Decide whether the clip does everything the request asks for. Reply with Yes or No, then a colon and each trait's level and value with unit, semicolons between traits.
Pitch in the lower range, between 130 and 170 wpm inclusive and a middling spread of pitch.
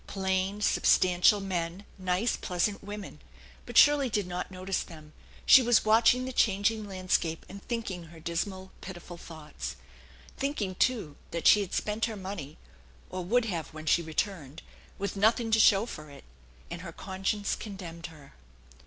No: high, 190 Hz; average, 155 wpm; average, 3.7 semitones